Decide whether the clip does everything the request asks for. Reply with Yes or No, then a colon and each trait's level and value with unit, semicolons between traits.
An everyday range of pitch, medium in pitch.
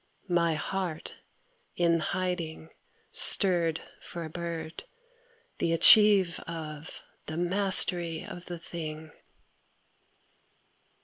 No: narrow, 1.9 semitones; medium, 170 Hz